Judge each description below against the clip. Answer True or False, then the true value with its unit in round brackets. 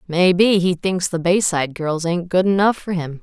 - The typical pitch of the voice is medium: True (180 Hz)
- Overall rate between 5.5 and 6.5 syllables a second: False (4.9 syllables/s)